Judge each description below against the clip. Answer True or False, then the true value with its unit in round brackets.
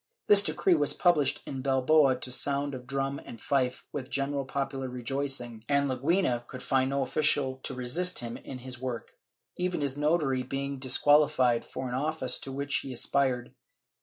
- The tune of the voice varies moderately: False (2.0 semitones)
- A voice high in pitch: False (135 Hz)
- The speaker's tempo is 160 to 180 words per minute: True (170 wpm)